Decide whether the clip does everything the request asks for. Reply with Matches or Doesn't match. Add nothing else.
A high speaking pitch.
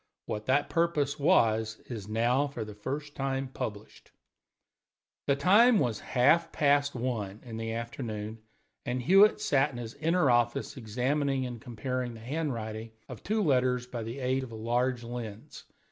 Doesn't match